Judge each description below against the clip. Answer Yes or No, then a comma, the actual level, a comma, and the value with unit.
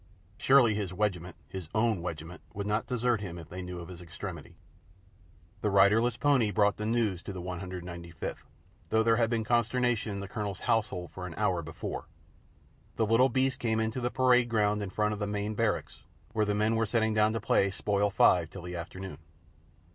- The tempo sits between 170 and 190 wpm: No, average, 200 wpm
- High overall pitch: No, low, 105 Hz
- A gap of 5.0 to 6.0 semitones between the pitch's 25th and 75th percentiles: No, average, 3.6 semitones